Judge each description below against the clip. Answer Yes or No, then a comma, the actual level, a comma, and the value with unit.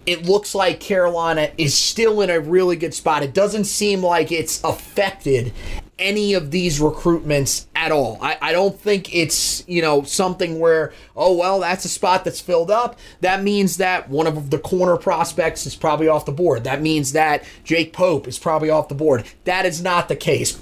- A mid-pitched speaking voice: Yes, medium, 170 Hz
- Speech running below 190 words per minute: No, average, 200 wpm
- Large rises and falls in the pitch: No, average, 3.3 semitones